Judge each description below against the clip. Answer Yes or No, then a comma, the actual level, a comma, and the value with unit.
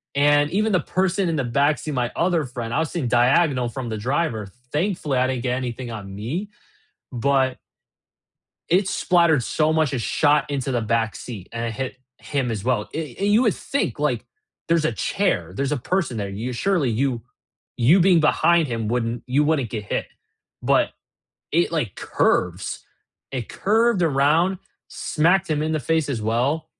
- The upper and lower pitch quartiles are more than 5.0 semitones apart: Yes, wide, 5.6 semitones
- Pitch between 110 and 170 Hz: Yes, medium, 140 Hz